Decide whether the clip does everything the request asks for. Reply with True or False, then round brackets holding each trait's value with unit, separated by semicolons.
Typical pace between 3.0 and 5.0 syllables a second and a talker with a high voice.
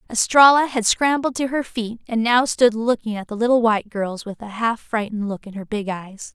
False (5.3 syllables/s; 225 Hz)